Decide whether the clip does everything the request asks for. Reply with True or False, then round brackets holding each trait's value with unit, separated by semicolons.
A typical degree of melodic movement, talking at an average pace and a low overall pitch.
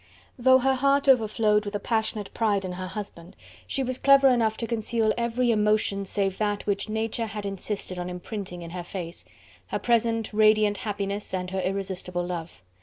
False (3.2 semitones; 180 wpm; 210 Hz)